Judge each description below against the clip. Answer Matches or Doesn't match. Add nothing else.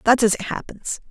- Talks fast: Matches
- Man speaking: Doesn't match